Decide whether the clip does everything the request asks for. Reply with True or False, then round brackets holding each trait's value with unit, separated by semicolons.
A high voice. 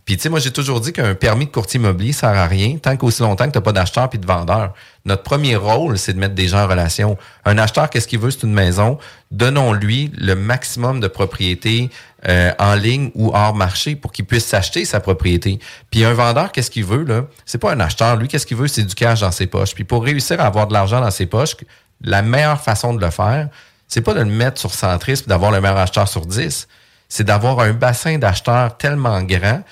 False (115 Hz)